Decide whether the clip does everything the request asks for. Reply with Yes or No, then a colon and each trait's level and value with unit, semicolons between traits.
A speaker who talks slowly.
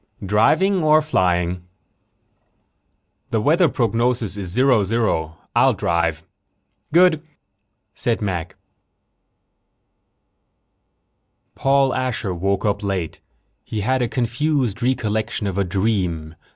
Yes: slow, 100 wpm